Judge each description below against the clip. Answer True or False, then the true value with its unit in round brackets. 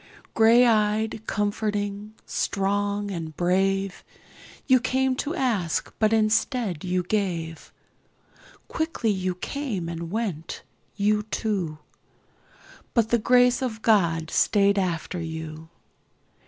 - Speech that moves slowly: True (100 wpm)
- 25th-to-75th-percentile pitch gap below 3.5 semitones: False (3.8 semitones)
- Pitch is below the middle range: False (205 Hz)